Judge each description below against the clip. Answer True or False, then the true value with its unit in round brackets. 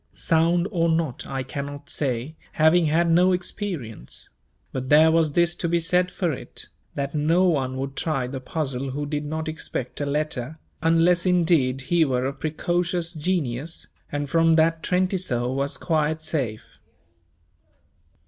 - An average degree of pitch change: True (3.6 semitones)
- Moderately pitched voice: True (155 Hz)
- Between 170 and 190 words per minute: False (150 wpm)